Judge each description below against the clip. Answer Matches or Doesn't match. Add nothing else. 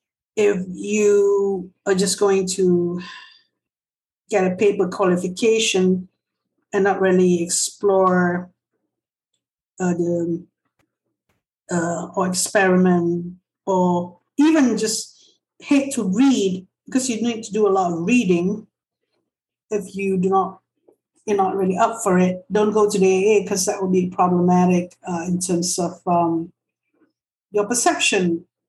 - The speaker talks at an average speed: Doesn't match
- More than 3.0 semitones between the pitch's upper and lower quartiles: Doesn't match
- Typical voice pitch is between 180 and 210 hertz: Matches